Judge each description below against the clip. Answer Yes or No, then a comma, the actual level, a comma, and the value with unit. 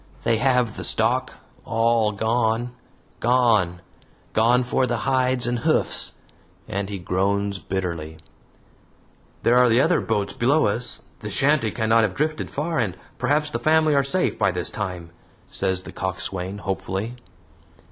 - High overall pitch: No, low, 115 Hz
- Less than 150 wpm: Yes, average, 140 wpm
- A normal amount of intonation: Yes, average, 4.3 semitones